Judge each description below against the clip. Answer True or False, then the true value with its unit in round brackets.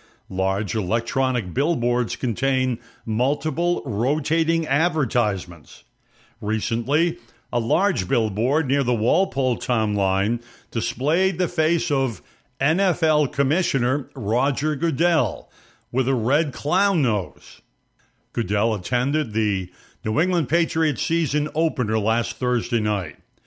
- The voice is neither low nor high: False (125 Hz)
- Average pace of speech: False (100 wpm)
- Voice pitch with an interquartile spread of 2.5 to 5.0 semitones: False (5.4 semitones)